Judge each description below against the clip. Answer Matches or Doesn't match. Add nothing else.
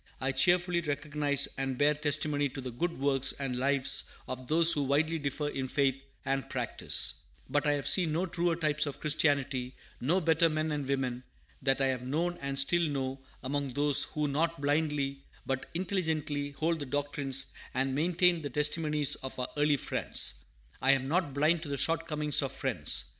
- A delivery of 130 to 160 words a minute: Doesn't match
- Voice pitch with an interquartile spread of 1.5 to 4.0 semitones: Matches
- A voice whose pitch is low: Doesn't match